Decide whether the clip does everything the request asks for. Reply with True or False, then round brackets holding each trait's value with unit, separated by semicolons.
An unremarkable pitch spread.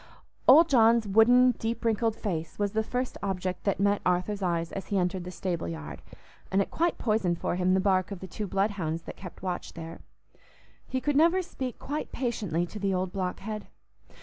True (3.8 semitones)